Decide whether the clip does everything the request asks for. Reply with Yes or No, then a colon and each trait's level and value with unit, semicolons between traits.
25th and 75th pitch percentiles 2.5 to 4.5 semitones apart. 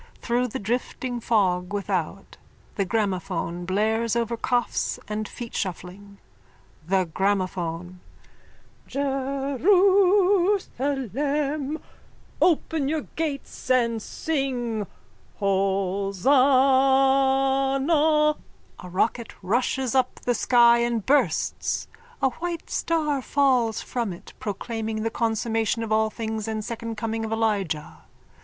No: average, 5.0 semitones